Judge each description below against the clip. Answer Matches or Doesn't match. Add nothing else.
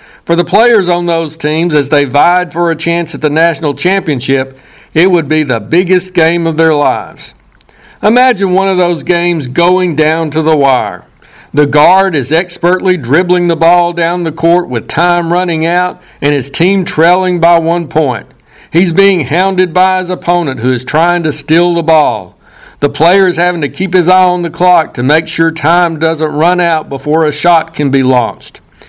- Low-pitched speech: Doesn't match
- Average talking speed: Matches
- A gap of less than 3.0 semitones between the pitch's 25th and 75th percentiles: Matches